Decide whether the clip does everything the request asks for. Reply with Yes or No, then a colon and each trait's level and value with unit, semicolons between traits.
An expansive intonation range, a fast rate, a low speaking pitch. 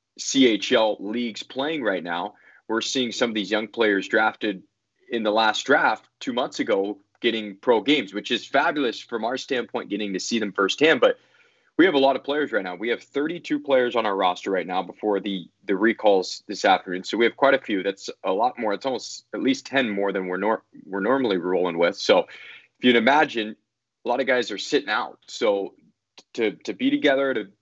Yes: wide, 5.7 semitones; fast, 215 wpm; low, 115 Hz